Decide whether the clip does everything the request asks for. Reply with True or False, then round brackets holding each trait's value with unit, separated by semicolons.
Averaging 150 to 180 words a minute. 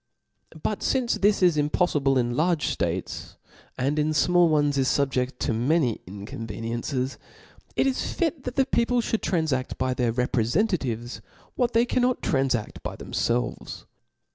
False (140 wpm)